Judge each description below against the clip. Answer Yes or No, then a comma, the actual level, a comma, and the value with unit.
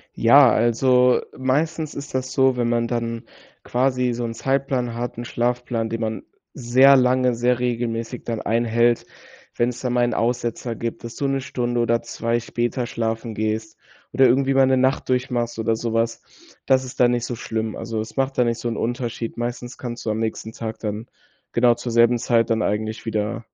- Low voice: Yes, low, 120 Hz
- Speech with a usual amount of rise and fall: No, narrow, 1.7 semitones